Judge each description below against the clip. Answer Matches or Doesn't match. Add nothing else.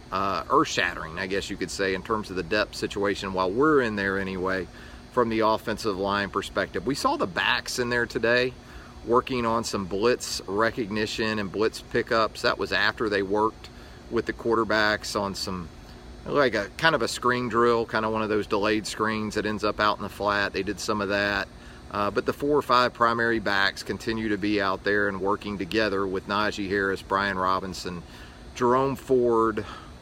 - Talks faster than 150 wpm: Matches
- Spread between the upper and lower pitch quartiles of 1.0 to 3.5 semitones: Matches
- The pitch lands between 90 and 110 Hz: Matches